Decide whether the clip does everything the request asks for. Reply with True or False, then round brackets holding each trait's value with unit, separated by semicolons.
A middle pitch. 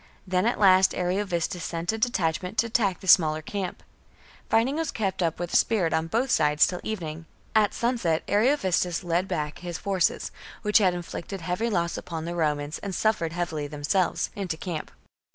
True (180 Hz)